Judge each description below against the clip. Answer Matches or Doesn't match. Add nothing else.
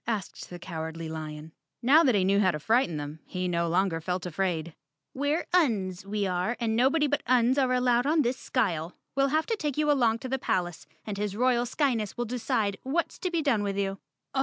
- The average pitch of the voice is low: Doesn't match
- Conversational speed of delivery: Doesn't match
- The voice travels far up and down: Matches